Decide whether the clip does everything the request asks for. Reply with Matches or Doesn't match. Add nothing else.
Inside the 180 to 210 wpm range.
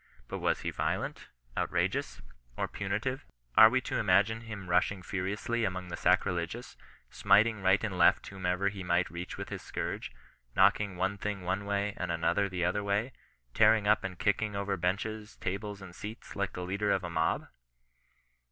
Doesn't match